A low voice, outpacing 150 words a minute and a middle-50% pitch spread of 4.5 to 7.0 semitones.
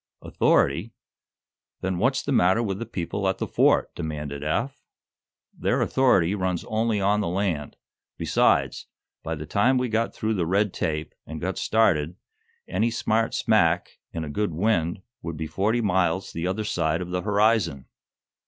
Yes: very low, 95 Hz; average, 160 wpm; average, 4.8 semitones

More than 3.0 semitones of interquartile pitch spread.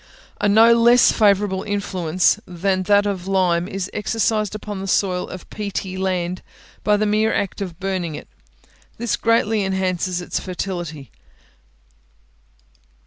No: narrow, 2.4 semitones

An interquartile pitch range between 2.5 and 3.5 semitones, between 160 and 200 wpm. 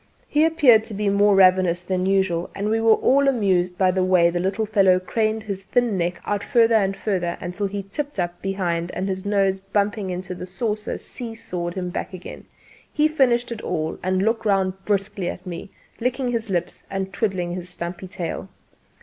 Yes: average, 3.2 semitones; average, 195 wpm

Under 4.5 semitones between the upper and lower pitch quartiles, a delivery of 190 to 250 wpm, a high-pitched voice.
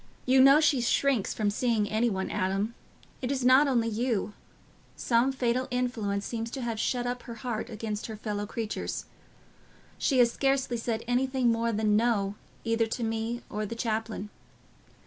No: narrow, 2.6 semitones; average, 165 wpm; high, 230 Hz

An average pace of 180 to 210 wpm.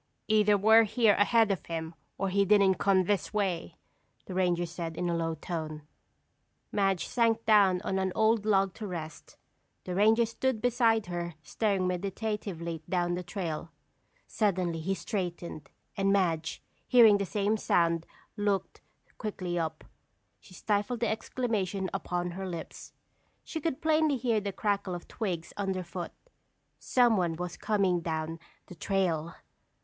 No: average, 145 wpm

